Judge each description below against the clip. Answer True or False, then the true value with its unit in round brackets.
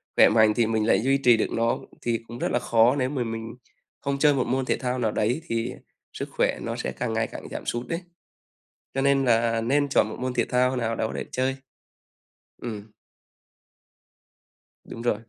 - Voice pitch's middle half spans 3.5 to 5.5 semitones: False (2.5 semitones)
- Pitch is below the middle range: True (120 Hz)